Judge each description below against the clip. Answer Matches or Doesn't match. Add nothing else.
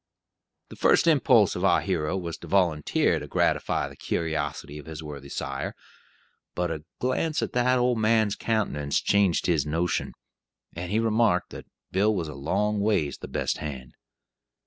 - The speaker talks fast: Doesn't match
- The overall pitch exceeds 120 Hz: Doesn't match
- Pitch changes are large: Matches